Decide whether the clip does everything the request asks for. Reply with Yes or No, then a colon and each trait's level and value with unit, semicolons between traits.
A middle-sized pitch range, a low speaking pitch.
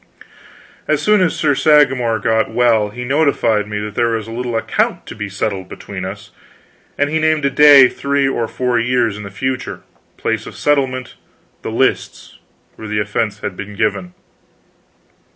Yes: average, 4.6 semitones; low, 120 Hz